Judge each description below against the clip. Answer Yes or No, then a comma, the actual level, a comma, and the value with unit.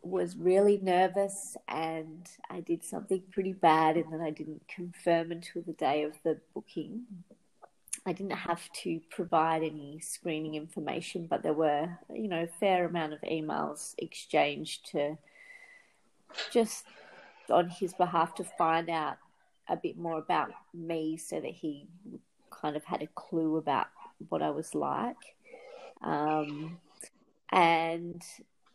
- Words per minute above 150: No, average, 140 wpm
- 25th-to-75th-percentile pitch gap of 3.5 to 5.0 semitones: No, average, 3.0 semitones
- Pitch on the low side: No, medium, 170 Hz